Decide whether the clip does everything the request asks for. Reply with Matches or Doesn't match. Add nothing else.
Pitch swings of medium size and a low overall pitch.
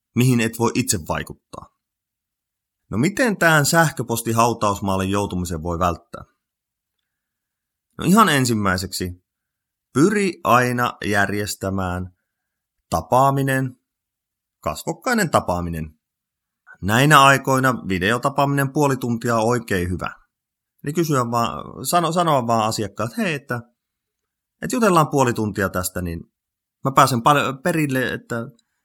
Doesn't match